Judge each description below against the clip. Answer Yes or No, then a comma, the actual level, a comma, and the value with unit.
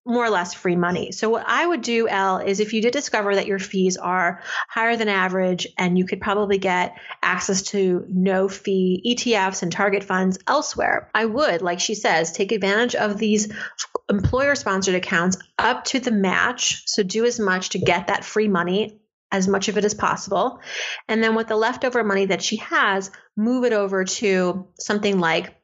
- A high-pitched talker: Yes, high, 200 Hz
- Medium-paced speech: Yes, average, 195 wpm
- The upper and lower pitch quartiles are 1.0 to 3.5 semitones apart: Yes, average, 3.0 semitones